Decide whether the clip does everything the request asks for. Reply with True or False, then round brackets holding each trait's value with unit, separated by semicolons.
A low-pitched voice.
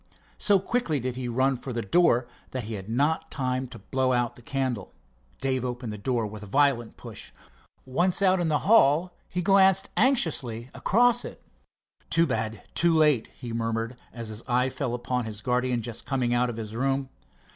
True (130 Hz)